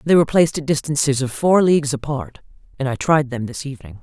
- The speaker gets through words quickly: Yes, fast, 225 wpm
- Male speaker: No, female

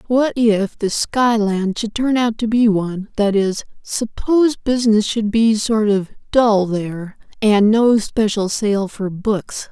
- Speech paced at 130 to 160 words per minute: Yes, average, 155 wpm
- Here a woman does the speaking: Yes, female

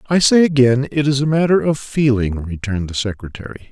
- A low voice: Yes, low, 130 Hz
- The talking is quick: No, average, 195 wpm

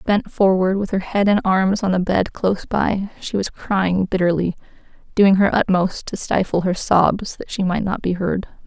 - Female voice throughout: Yes, female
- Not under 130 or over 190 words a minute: No, average, 200 wpm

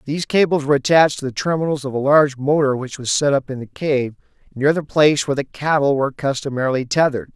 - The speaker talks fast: Yes, fast, 220 wpm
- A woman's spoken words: No, male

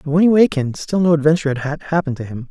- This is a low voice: No, medium, 155 Hz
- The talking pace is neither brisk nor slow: No, fast, 265 wpm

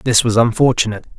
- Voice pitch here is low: Yes, low, 115 Hz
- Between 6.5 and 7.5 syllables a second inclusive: Yes, 6.6 syllables/s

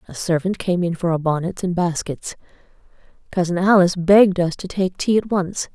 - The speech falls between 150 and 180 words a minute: No, average, 190 wpm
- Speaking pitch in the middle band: Yes, medium, 180 Hz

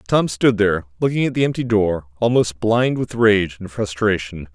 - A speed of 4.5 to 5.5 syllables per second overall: Yes, 4.9 syllables/s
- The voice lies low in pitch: Yes, low, 105 Hz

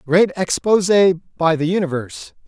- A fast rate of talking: No, slow, 120 wpm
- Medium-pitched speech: Yes, medium, 175 Hz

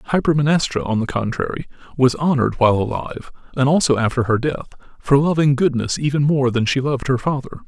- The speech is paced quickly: No, average, 180 wpm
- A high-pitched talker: No, low, 135 Hz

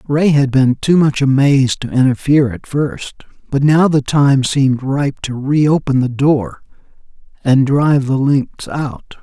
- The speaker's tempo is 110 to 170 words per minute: Yes, average, 165 wpm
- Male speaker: Yes, male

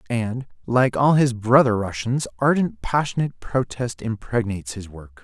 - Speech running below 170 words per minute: Yes, average, 140 wpm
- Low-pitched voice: Yes, low, 120 Hz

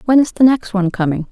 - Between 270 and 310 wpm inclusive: Yes, fast, 275 wpm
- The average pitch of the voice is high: Yes, high, 210 Hz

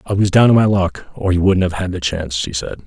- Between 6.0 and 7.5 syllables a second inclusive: Yes, 6.3 syllables/s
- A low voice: Yes, very low, 90 Hz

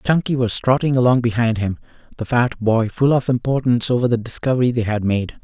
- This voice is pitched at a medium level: No, low, 120 Hz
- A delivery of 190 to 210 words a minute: Yes, average, 200 wpm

